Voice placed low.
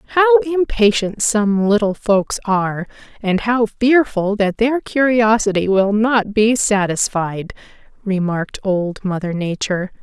No: high, 215 Hz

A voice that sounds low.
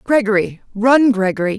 No: high, 220 Hz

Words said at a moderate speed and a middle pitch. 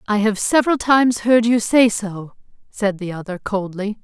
No: average, 180 wpm; high, 215 Hz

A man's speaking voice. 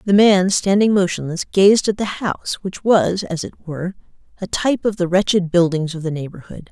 No: female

